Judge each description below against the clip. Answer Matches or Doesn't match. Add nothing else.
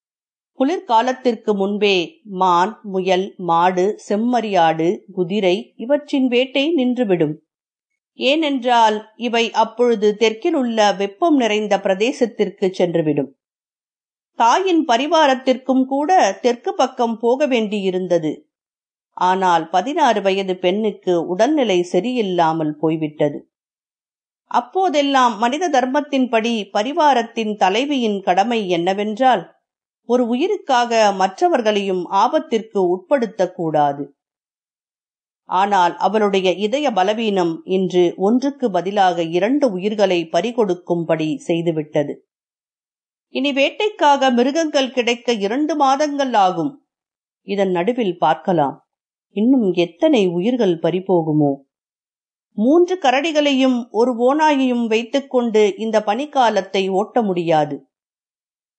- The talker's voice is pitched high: Matches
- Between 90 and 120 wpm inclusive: Doesn't match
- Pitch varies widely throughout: Matches